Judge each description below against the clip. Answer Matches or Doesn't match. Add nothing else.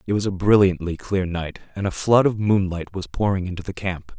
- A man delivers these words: Matches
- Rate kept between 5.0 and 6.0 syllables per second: Matches